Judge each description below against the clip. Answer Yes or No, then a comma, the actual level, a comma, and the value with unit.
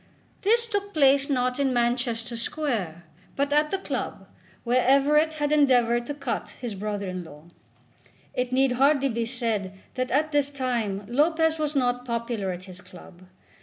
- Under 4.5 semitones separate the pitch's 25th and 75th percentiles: Yes, average, 4.0 semitones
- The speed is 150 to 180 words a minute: Yes, average, 165 wpm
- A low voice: No, very high, 250 Hz